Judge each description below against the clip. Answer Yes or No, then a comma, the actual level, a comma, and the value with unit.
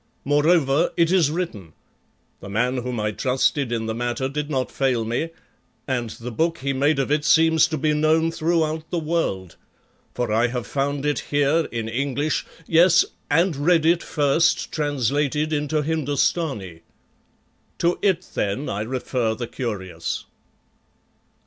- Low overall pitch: No, medium, 145 Hz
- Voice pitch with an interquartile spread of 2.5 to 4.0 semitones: No, average, 4.7 semitones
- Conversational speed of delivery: Yes, average, 150 wpm